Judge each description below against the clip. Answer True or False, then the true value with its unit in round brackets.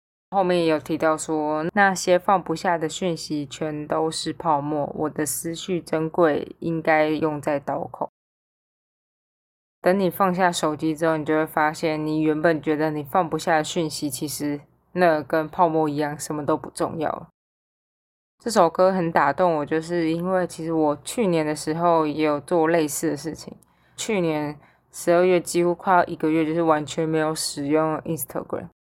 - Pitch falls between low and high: True (160 Hz)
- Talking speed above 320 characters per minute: False (260 characters per minute)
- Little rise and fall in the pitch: True (2.0 semitones)